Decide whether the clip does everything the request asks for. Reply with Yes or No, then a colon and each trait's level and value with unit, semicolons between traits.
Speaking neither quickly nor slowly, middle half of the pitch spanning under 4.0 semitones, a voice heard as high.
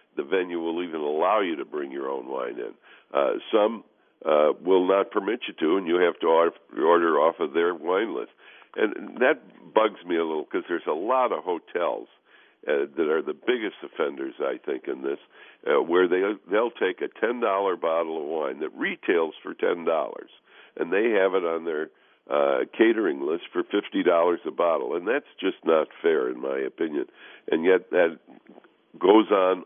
Yes: average, 190 wpm; average, 3.5 semitones; very high, 400 Hz